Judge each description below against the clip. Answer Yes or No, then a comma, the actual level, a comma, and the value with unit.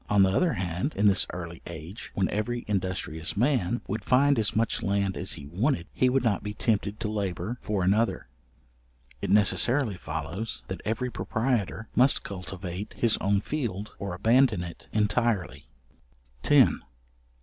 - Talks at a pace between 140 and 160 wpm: Yes, average, 155 wpm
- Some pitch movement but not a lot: Yes, average, 4.1 semitones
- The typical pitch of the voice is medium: No, low, 105 Hz